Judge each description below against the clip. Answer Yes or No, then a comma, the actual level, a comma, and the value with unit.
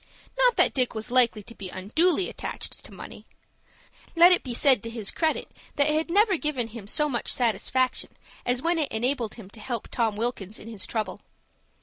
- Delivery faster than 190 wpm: Yes, average, 200 wpm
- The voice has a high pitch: Yes, high, 245 Hz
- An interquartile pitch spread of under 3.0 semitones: No, wide, 5.5 semitones